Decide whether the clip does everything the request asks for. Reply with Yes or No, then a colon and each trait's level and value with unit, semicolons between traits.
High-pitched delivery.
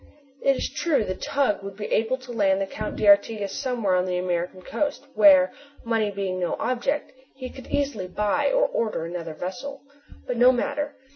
Yes: high, 220 Hz